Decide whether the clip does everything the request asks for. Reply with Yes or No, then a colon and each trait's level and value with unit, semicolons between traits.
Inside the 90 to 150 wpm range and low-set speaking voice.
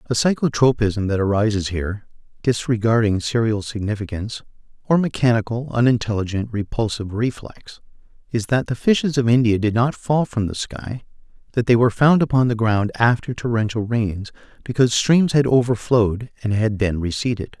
Yes: average, 140 wpm; low, 115 Hz